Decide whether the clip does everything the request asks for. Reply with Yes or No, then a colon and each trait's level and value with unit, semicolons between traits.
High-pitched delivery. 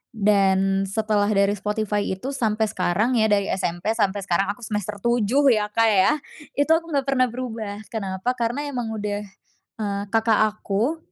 Yes: high, 215 Hz